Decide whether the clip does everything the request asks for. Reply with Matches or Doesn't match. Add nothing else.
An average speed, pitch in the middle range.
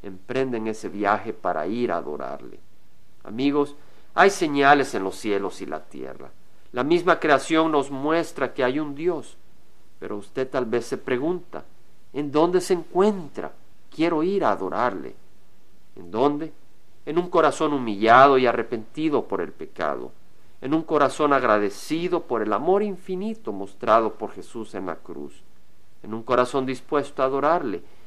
Matches